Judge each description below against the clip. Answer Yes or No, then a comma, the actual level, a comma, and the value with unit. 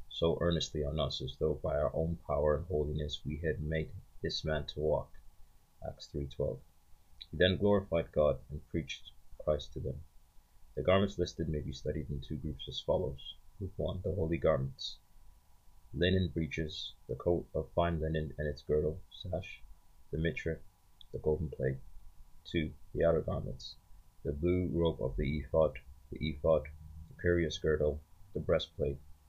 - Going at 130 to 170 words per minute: Yes, average, 160 wpm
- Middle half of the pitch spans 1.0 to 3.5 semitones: Yes, average, 2.8 semitones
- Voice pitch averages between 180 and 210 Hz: No, very low, 80 Hz